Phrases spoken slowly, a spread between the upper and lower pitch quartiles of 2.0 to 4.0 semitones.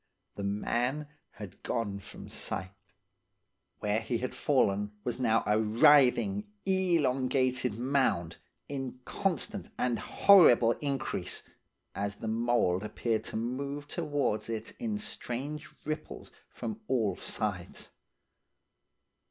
No: slow, 110 wpm; average, 5.3 semitones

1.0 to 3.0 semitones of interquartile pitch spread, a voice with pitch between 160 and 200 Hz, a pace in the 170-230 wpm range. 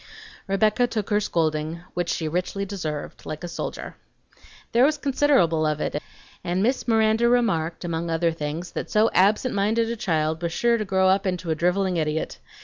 No: average, 5.0 semitones; medium, 185 Hz; average, 180 wpm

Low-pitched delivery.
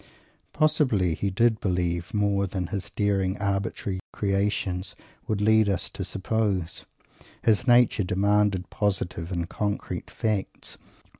Yes: low, 100 Hz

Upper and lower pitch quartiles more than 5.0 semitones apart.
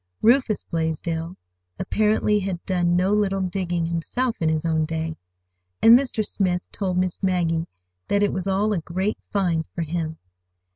No: average, 3.5 semitones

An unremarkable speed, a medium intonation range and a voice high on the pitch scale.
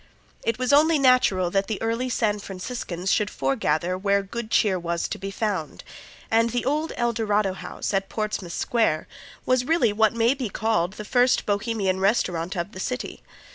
Yes: average, 175 wpm; average, 4.1 semitones; high, 210 Hz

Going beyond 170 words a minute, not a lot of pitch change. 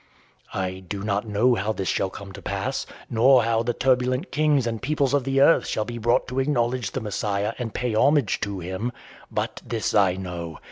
No: average, 195 wpm; average, 4.2 semitones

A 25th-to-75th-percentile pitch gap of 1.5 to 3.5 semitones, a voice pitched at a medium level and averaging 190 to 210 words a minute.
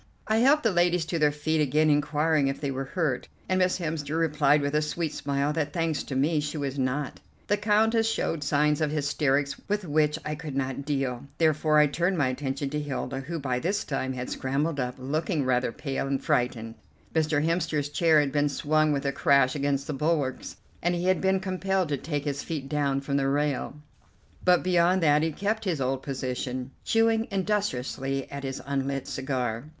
Yes: average, 3.2 semitones; medium, 150 Hz; average, 195 wpm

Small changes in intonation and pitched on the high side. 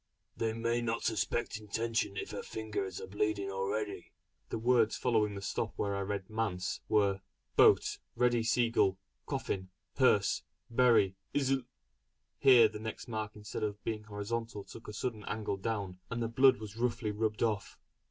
No: narrow, 2.3 semitones; low, 110 Hz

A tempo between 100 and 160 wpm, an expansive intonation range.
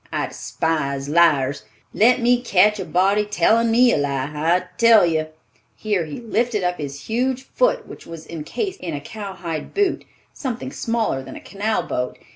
No: average, 170 wpm; wide, 7.0 semitones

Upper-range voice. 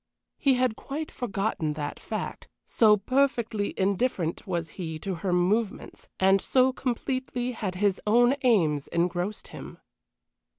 Yes: high, 205 Hz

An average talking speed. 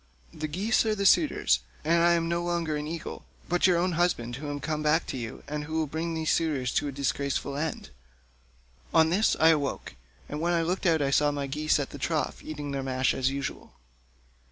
No: fast, 220 wpm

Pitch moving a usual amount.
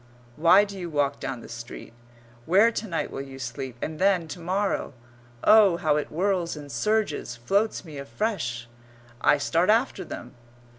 No: wide, 6.4 semitones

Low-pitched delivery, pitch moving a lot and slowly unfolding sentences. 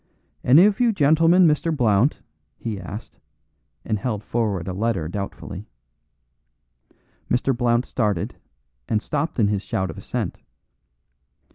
Yes: low, 115 Hz; wide, 6.7 semitones; slow, 125 wpm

